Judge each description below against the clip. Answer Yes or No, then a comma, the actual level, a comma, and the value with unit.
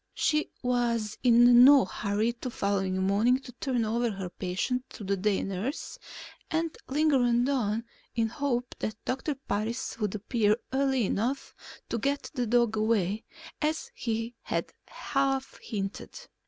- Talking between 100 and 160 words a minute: Yes, average, 145 wpm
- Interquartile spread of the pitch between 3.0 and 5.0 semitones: Yes, average, 3.9 semitones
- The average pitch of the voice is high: Yes, high, 235 Hz